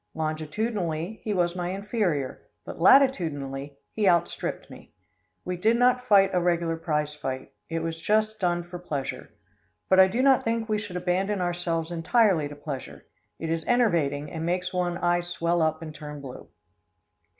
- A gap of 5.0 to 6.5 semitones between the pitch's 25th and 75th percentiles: No, average, 4.2 semitones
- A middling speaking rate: Yes, average, 165 wpm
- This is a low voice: No, medium, 175 Hz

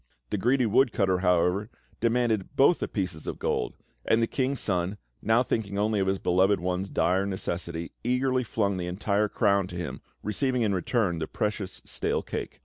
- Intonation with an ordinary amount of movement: Yes, average, 3.8 semitones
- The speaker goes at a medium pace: Yes, average, 175 wpm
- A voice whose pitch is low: Yes, low, 100 Hz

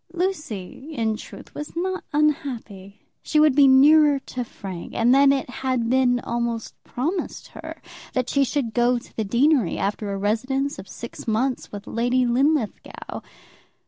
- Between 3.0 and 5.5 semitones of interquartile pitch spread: Yes, average, 4.1 semitones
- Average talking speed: Yes, average, 155 wpm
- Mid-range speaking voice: No, very high, 255 Hz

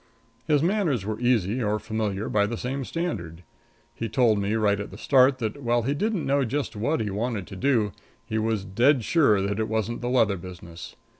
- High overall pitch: No, low, 115 Hz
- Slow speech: No, fast, 205 wpm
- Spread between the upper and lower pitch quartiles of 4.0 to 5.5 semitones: Yes, average, 4.3 semitones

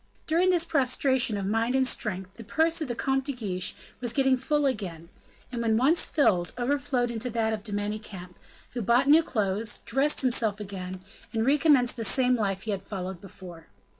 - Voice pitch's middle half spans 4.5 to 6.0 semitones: Yes, average, 4.9 semitones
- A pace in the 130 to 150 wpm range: No, average, 190 wpm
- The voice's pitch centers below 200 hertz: No, high, 235 Hz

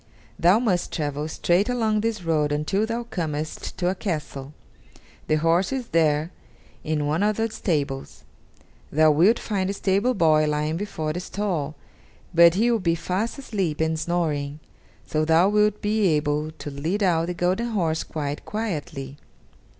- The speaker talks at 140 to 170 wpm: Yes, average, 160 wpm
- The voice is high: No, medium, 170 Hz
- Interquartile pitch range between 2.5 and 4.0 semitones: No, average, 5.1 semitones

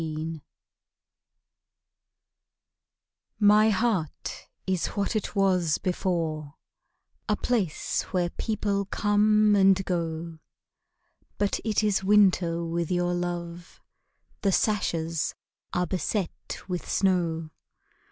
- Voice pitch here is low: No, medium, 180 Hz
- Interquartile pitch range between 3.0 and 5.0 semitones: Yes, average, 3.4 semitones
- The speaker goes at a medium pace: No, slow, 95 wpm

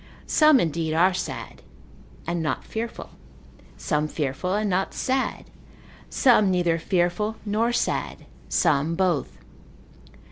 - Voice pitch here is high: No, medium, 180 Hz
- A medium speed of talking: No, slow, 110 wpm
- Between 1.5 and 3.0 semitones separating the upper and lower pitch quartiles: No, average, 4.7 semitones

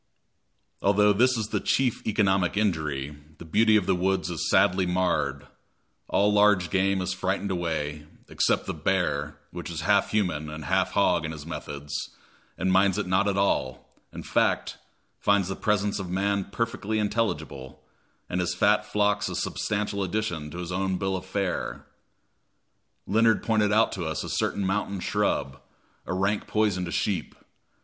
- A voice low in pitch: Yes, very low, 95 Hz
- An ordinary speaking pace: Yes, average, 165 wpm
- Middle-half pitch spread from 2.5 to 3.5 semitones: Yes, average, 3.1 semitones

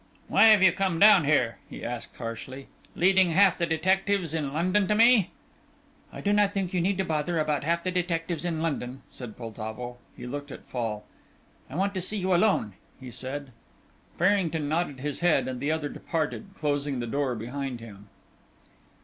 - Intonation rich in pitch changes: Yes, wide, 6.0 semitones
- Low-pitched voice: No, medium, 160 Hz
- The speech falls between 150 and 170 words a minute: No, average, 180 wpm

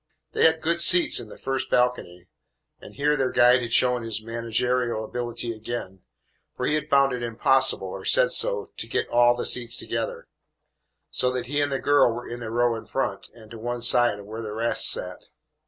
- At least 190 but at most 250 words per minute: Yes, fast, 205 wpm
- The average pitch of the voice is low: Yes, low, 120 Hz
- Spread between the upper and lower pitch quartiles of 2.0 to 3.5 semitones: Yes, narrow, 2.6 semitones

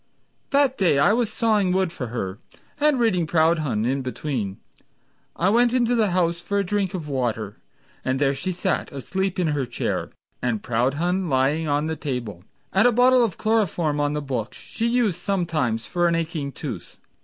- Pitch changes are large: Yes, wide, 6.8 semitones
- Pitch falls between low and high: Yes, medium, 165 Hz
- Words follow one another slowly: No, average, 180 wpm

